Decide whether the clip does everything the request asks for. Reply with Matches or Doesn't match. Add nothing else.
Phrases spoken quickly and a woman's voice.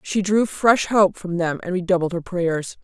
Matches